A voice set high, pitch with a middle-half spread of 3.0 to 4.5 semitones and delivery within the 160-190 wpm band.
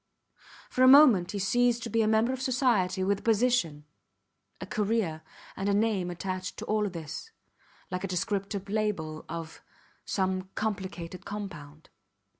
No: high, 200 Hz; average, 3.6 semitones; average, 150 wpm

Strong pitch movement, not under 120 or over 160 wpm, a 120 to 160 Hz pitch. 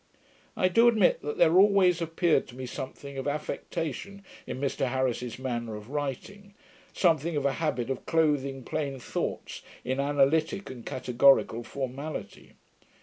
No: average, 4.0 semitones; average, 145 wpm; medium, 140 Hz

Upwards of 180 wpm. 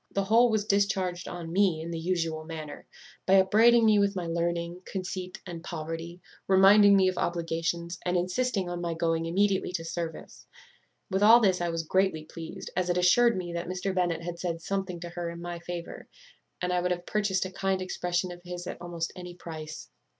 Yes: average, 200 wpm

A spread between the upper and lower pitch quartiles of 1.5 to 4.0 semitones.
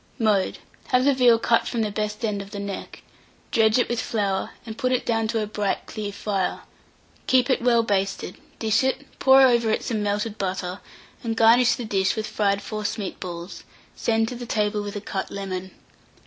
Yes: narrow, 2.6 semitones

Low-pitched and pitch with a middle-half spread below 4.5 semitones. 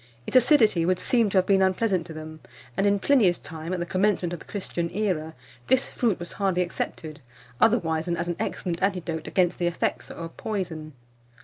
No: medium, 180 Hz; average, 3.3 semitones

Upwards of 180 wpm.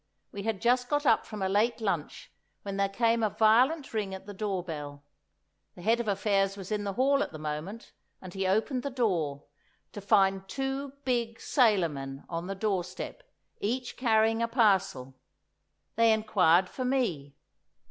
No: average, 170 wpm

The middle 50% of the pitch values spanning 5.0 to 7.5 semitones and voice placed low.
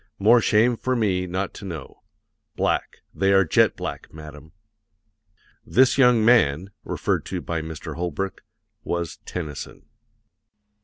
Yes: average, 5.3 semitones; very low, 95 Hz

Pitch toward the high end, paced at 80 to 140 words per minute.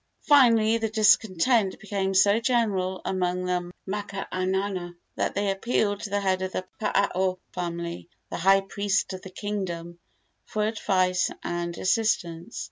Yes: high, 195 Hz; slow, 135 wpm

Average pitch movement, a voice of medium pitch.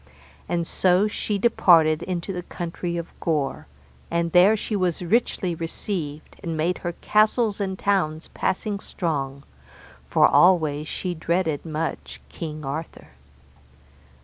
Yes: average, 3.0 semitones; medium, 170 Hz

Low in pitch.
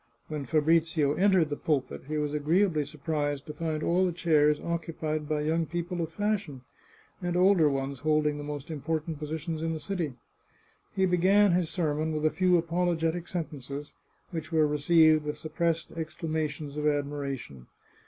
No: medium, 155 Hz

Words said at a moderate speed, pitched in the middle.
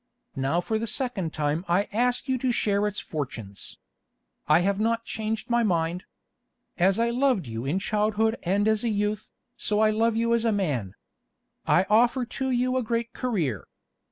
No: average, 180 wpm; high, 215 Hz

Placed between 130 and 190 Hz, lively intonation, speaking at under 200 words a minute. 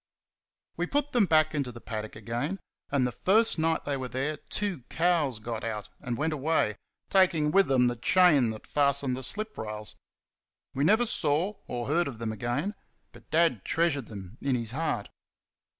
Yes: medium, 140 Hz; wide, 5.9 semitones; average, 180 wpm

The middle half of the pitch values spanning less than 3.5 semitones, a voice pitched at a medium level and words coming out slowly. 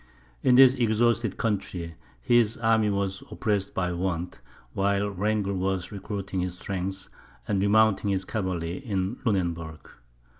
No: average, 2.8 semitones; low, 100 Hz; slow, 125 wpm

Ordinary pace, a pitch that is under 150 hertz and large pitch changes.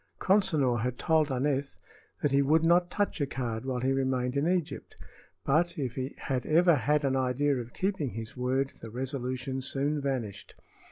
No: average, 175 wpm; low, 135 Hz; average, 3.1 semitones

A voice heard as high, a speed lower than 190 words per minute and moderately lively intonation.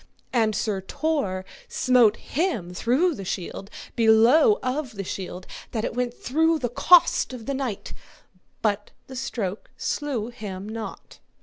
Yes: high, 235 Hz; average, 140 wpm; average, 4.6 semitones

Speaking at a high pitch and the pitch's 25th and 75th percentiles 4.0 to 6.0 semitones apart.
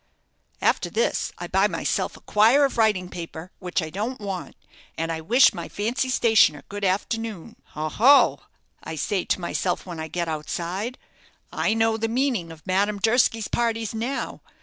Yes: high, 205 Hz; average, 4.8 semitones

